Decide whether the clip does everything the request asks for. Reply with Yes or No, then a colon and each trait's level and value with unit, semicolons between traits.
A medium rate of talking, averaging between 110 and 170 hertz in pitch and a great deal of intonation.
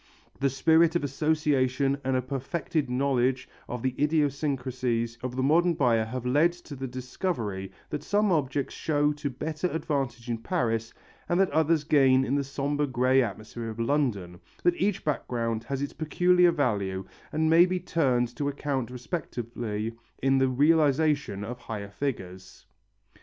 No: average, 155 wpm; low, 135 Hz; average, 4.1 semitones